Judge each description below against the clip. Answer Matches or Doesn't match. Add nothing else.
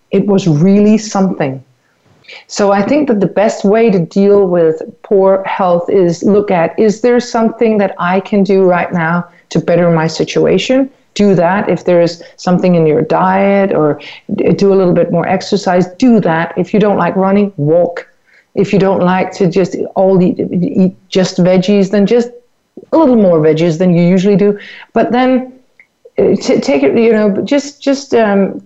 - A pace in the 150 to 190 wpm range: Matches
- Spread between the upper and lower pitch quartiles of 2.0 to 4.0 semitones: Matches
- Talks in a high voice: Matches